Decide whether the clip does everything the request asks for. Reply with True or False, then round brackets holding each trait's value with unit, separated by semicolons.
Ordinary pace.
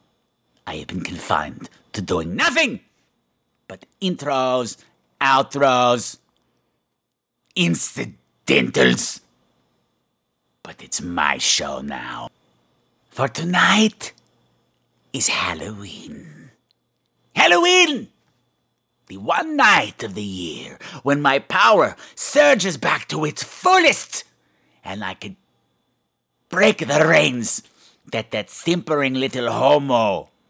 False (90 wpm)